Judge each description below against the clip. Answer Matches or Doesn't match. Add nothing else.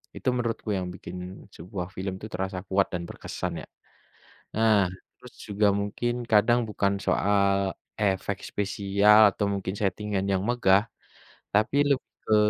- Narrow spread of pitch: Matches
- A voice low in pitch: Matches